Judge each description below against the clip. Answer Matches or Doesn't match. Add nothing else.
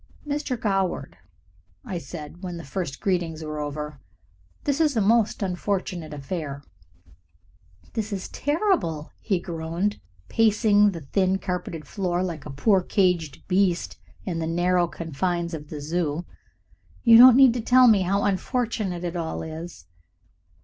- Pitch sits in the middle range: Matches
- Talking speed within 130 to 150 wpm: Matches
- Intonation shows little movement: Doesn't match